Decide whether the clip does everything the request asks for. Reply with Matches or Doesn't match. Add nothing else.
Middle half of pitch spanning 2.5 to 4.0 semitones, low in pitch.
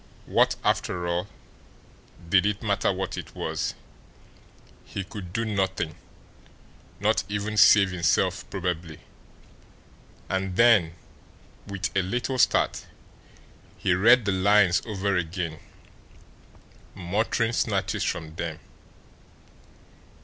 Matches